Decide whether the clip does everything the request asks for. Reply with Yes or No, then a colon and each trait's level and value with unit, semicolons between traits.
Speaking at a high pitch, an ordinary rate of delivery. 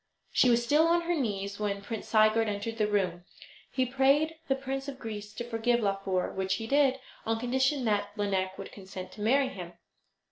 Yes: high, 225 Hz; average, 190 wpm